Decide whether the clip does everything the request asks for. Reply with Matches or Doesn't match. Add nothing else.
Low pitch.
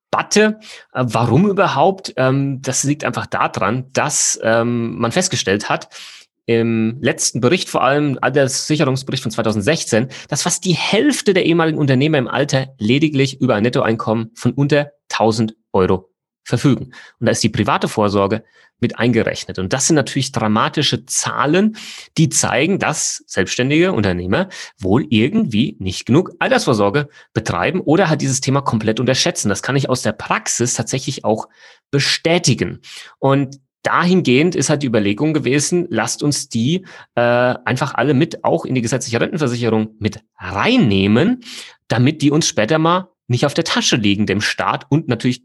Matches